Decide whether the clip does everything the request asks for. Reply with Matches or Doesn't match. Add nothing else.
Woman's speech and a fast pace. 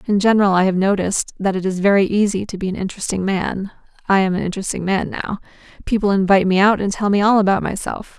Matches